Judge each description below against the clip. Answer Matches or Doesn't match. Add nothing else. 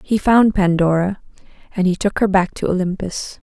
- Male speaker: Doesn't match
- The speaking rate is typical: Matches